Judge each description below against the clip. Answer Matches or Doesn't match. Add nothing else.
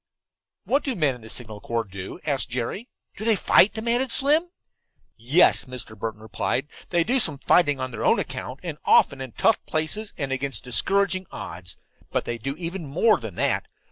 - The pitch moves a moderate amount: Doesn't match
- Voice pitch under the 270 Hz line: Matches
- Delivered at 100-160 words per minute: Doesn't match